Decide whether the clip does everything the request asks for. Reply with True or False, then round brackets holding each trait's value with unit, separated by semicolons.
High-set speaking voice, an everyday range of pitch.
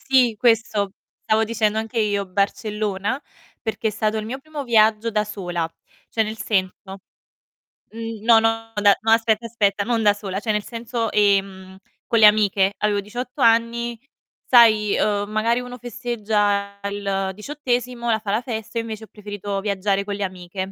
False (215 Hz; 2.2 semitones)